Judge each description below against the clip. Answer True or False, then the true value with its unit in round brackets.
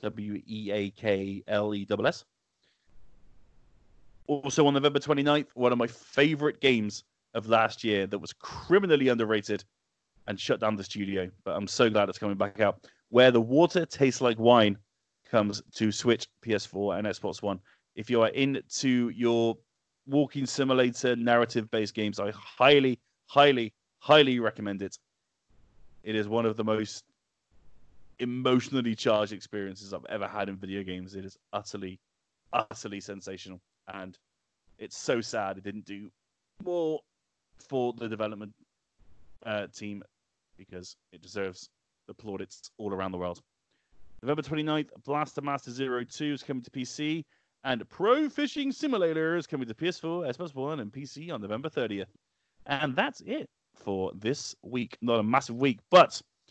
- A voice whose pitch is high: False (115 Hz)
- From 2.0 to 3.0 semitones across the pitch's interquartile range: False (5.3 semitones)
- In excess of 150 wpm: False (145 wpm)